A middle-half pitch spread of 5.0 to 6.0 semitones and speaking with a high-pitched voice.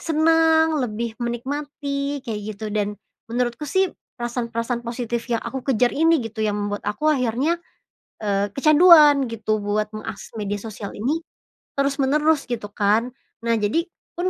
Yes: average, 5.3 semitones; high, 240 Hz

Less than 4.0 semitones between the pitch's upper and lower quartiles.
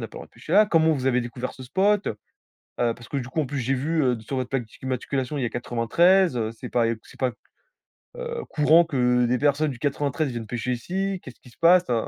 No: average, 4.7 semitones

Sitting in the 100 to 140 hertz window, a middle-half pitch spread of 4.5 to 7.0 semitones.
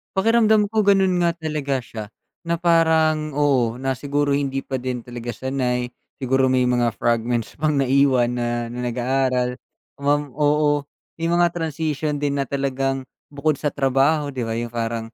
No: low, 135 Hz; average, 3.6 semitones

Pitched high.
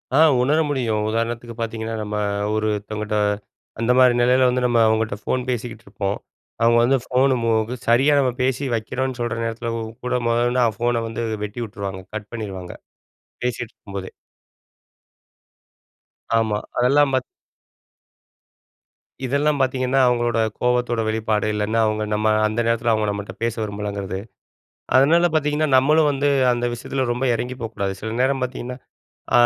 No: low, 120 Hz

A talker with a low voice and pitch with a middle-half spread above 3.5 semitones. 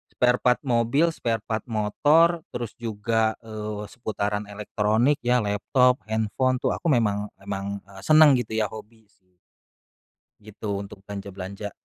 No: low, 110 Hz; average, 3.1 semitones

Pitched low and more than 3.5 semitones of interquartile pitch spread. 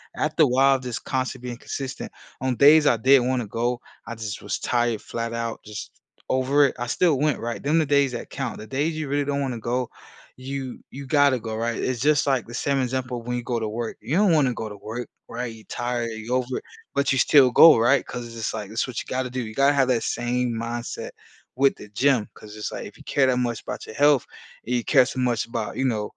No: low, 125 Hz; average, 2.8 semitones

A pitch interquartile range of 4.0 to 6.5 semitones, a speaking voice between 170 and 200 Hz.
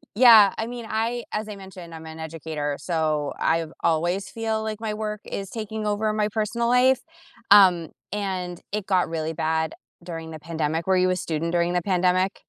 Yes: average, 4.7 semitones; medium, 185 Hz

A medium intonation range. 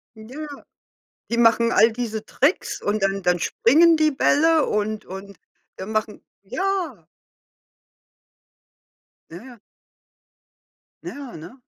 No: wide, 5.8 semitones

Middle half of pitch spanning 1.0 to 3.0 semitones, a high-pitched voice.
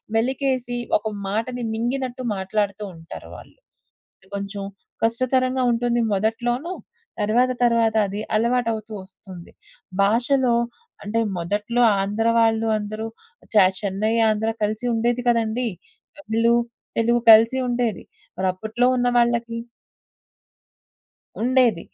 Yes: narrow, 2.5 semitones; high, 230 Hz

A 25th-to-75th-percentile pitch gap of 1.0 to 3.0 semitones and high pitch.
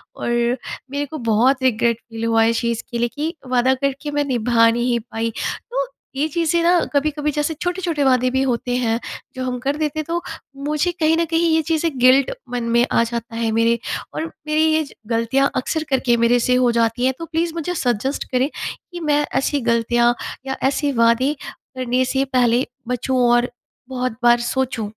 No: average, 3.9 semitones; very high, 255 Hz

